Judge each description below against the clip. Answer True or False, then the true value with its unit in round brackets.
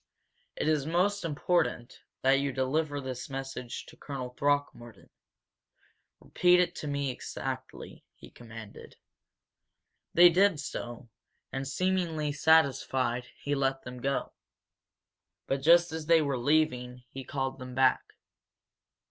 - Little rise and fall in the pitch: False (3.8 semitones)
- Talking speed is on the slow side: True (125 wpm)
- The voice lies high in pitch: False (140 Hz)